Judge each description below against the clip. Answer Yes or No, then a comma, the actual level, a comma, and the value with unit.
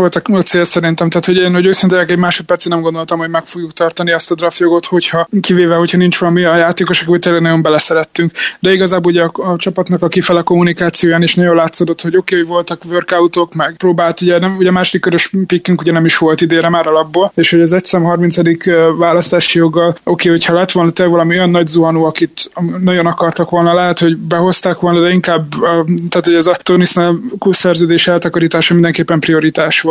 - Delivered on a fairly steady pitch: Yes, narrow, 1.1 semitones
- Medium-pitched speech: Yes, medium, 175 Hz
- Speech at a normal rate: No, fast, 205 wpm